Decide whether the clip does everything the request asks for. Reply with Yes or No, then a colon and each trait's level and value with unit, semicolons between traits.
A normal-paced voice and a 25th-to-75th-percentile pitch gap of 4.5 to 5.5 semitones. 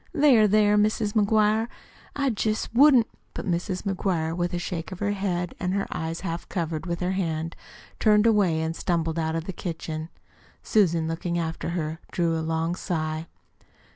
No: average, 175 wpm; average, 4.1 semitones